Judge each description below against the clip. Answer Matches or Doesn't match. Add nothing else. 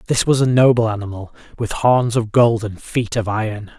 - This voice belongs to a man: Matches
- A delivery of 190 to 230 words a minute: Matches